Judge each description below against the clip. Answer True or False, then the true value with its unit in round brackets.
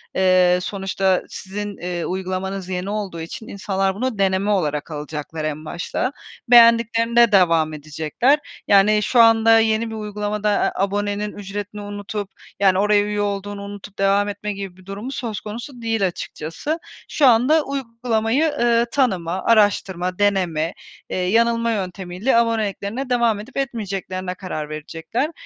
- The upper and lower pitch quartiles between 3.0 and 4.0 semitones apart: True (3.5 semitones)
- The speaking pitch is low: False (205 Hz)